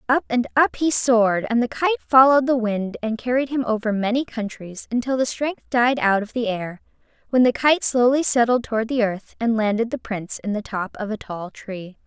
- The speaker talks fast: Yes, fast, 220 wpm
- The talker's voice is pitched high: Yes, high, 235 Hz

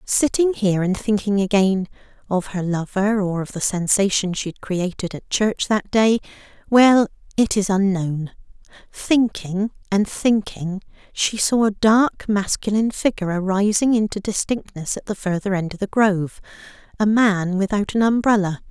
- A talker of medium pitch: No, high, 200 Hz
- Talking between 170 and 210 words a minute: No, average, 140 wpm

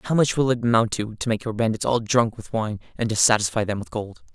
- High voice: No, low, 115 Hz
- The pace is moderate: No, fast, 275 wpm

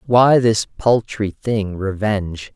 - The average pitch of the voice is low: Yes, low, 105 Hz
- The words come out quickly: No, slow, 115 wpm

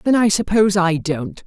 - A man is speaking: Yes, male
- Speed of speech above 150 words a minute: Yes, fast, 205 wpm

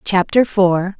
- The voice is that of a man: No, female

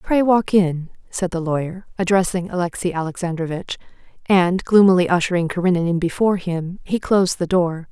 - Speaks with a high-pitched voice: No, medium, 180 Hz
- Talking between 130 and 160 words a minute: Yes, average, 150 wpm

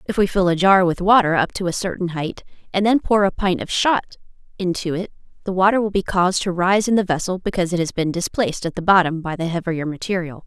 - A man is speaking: No, female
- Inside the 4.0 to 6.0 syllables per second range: No, 6.2 syllables/s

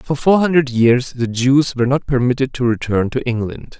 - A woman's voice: No, male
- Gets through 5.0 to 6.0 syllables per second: Yes, 5.1 syllables/s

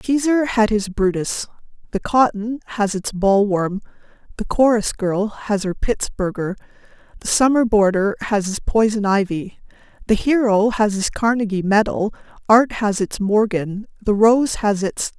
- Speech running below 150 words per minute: Yes, average, 140 wpm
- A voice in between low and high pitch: No, high, 210 Hz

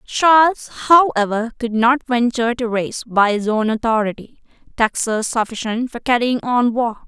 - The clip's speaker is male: No, female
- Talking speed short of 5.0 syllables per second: Yes, 4.7 syllables/s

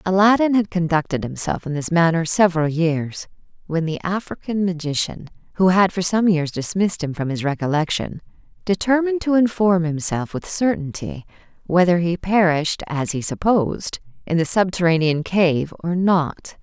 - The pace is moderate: Yes, average, 150 wpm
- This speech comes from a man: No, female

